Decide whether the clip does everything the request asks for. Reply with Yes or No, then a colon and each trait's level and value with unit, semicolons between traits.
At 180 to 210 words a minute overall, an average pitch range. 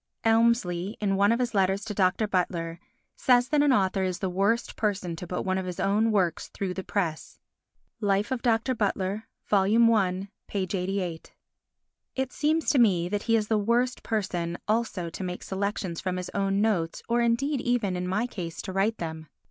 Yes: average, 185 wpm; average, 3.8 semitones